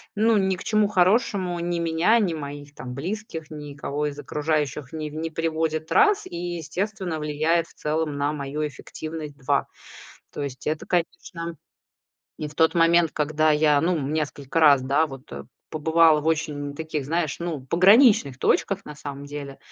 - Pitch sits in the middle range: Yes, medium, 155 Hz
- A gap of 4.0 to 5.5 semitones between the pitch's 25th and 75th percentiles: No, narrow, 2.6 semitones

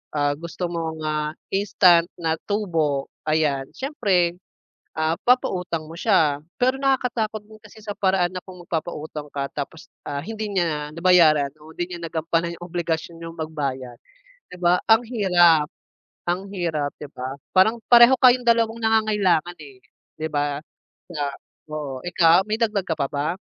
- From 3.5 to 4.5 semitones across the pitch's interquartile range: No, average, 4.9 semitones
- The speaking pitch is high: No, medium, 170 Hz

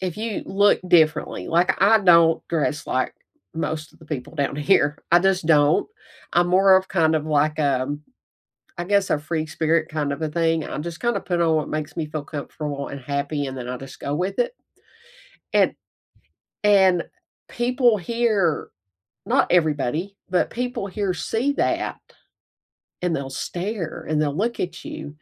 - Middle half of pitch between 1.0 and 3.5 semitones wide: No, average, 4.3 semitones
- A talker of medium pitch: Yes, medium, 165 Hz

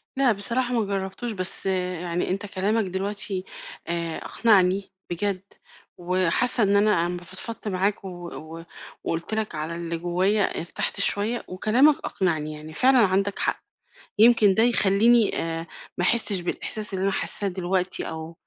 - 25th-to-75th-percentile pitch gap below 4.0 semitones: Yes, average, 3.4 semitones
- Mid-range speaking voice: No, high, 195 Hz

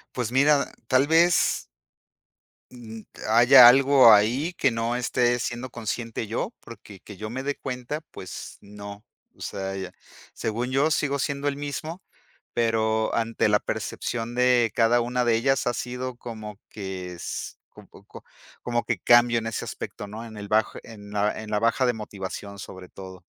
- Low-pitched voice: Yes, low, 115 Hz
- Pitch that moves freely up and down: No, average, 3.1 semitones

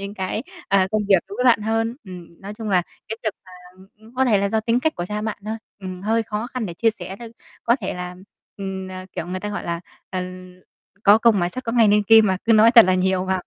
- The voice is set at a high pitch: Yes, high, 205 Hz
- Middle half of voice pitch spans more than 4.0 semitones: No, average, 3.1 semitones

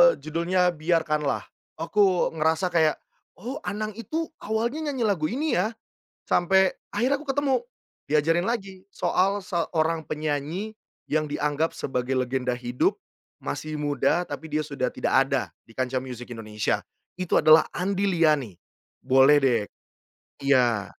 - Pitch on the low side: No, medium, 160 Hz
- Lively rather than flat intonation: Yes, wide, 5.7 semitones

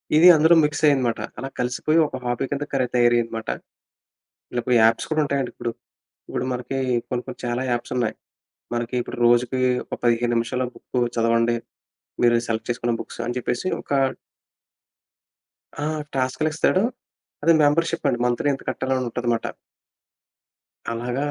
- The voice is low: Yes, low, 125 Hz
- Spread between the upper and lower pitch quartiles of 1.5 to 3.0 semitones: Yes, narrow, 2.4 semitones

